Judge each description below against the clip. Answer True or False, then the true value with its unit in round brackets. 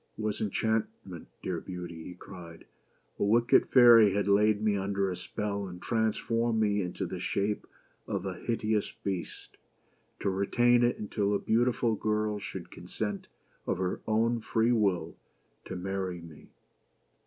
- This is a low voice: True (105 Hz)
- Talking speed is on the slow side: False (155 wpm)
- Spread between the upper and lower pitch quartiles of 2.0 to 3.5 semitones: True (2.7 semitones)